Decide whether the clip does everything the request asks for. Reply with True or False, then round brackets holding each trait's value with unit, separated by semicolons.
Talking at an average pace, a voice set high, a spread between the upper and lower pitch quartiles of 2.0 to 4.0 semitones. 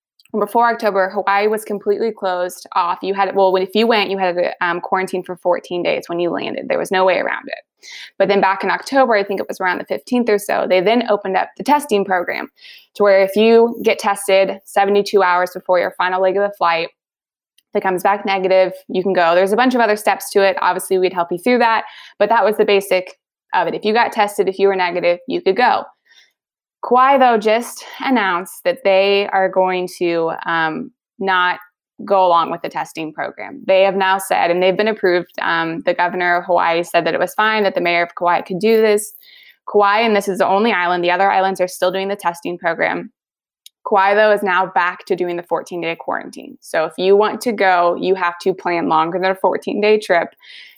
False (225 wpm; 195 Hz; 2.8 semitones)